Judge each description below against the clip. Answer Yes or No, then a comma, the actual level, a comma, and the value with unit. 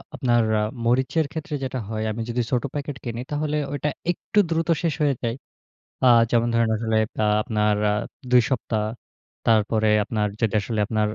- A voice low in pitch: Yes, low, 120 Hz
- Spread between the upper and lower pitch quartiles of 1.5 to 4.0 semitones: No, average, 4.6 semitones